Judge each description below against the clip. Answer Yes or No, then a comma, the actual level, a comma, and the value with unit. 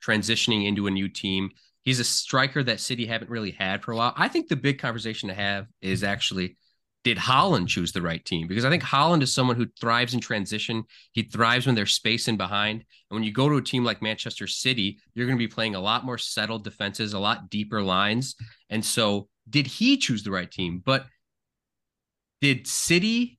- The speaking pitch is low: Yes, low, 110 Hz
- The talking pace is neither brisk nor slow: No, fast, 215 wpm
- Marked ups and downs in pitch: No, average, 3.6 semitones